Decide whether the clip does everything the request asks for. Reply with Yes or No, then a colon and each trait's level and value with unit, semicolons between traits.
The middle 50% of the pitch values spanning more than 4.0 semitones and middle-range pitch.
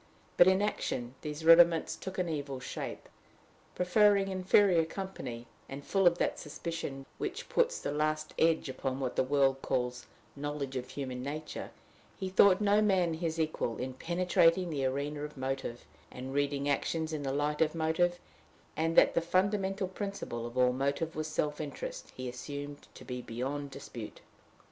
Yes: average, 4.6 semitones; medium, 150 Hz